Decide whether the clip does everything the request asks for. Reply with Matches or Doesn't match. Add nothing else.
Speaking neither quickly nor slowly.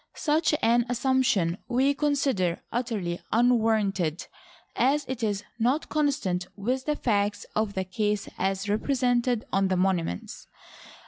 Doesn't match